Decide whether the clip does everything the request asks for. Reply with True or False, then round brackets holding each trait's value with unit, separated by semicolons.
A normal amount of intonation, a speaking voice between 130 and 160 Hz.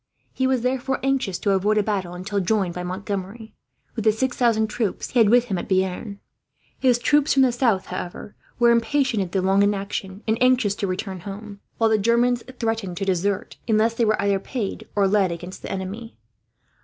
False (3.5 semitones; 210 Hz)